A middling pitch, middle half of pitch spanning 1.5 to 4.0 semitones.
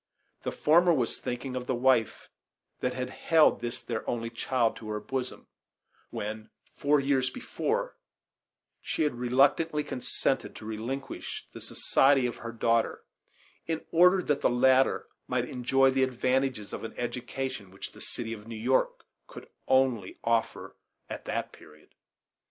No: low, 125 Hz; average, 2.7 semitones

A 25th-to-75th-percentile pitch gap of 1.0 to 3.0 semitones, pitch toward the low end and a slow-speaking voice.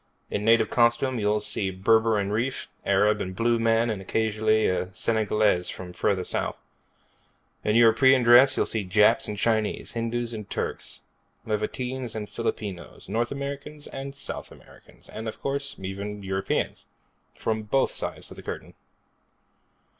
No: narrow, 2.4 semitones; low, 110 Hz; average, 145 wpm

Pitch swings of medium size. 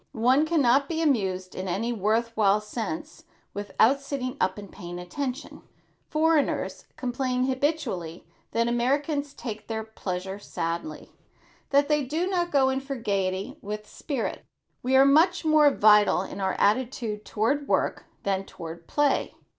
No: wide, 5.7 semitones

